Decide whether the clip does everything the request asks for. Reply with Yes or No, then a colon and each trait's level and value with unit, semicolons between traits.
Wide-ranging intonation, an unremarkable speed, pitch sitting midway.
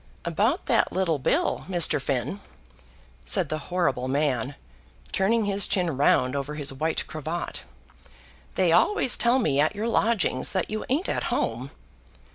Yes: wide, 6.8 semitones; average, 145 wpm; medium, 170 Hz